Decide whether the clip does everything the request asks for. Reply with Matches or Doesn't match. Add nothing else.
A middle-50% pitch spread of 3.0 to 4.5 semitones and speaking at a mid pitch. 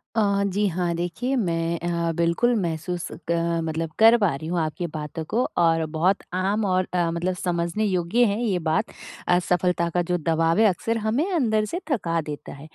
Matches